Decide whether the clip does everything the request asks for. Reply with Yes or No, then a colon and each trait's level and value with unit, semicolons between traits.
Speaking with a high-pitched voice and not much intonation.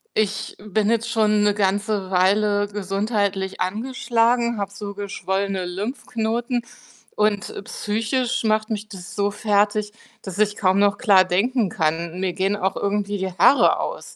Yes: high, 205 Hz; narrow, 2.0 semitones